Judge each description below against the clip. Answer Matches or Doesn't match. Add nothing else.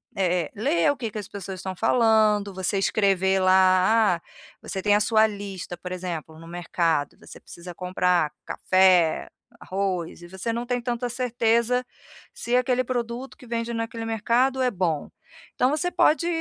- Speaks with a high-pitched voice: Matches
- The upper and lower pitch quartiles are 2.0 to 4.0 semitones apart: Doesn't match